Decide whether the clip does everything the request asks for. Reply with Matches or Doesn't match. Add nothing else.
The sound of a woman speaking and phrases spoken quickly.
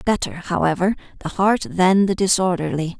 Doesn't match